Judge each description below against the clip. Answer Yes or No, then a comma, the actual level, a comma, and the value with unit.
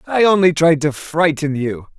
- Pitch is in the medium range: Yes, medium, 160 Hz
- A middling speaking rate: Yes, average, 180 wpm